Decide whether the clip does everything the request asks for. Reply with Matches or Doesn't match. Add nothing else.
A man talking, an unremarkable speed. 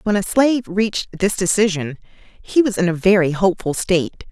Doesn't match